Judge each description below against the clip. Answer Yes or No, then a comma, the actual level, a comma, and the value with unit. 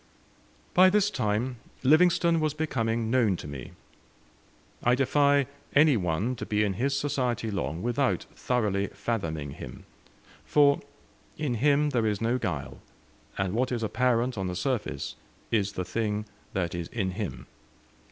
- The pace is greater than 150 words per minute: No, average, 145 wpm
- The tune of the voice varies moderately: No, wide, 5.7 semitones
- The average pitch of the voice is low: Yes, low, 115 Hz